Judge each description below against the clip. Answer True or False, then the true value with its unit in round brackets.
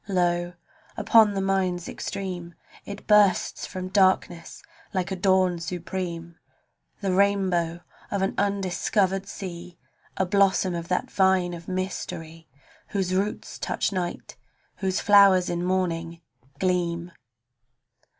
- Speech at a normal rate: False (120 wpm)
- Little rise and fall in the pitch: True (1.9 semitones)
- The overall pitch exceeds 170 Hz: True (185 Hz)